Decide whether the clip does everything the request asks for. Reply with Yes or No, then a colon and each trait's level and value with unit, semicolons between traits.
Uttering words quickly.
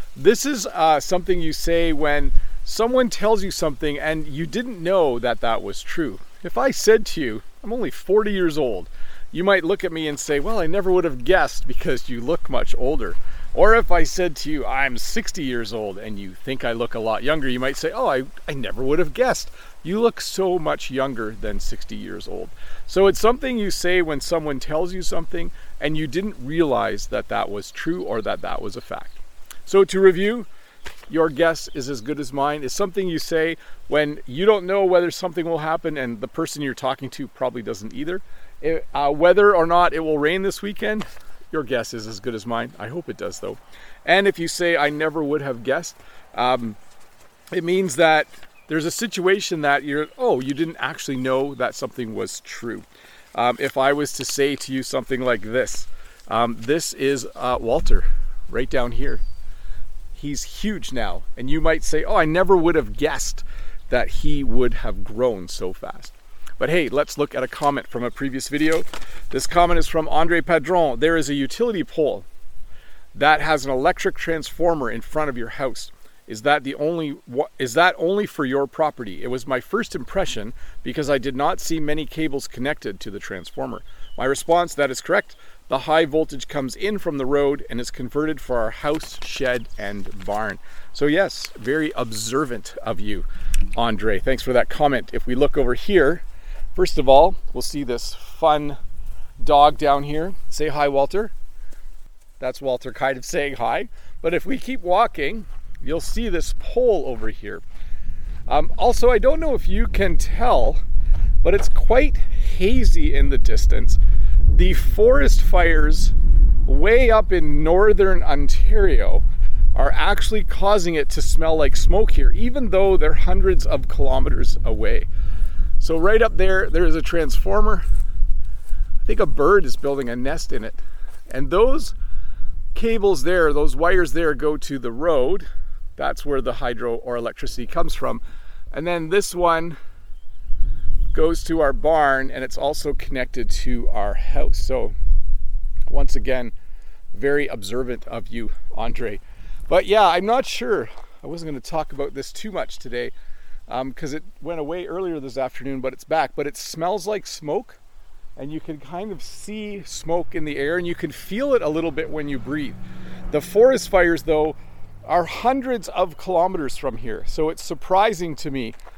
No: average, 185 wpm